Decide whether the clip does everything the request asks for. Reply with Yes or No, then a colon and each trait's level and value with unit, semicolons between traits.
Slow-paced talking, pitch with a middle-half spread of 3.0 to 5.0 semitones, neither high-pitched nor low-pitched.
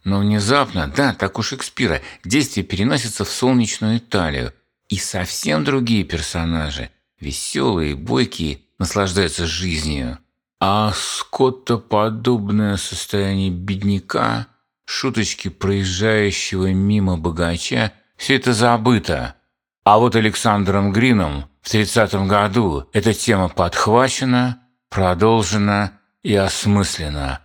No: slow, 95 wpm; average, 3.6 semitones; low, 100 Hz